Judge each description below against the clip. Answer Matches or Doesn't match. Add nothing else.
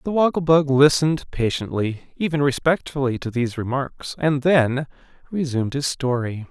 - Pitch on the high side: Doesn't match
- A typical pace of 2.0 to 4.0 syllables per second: Doesn't match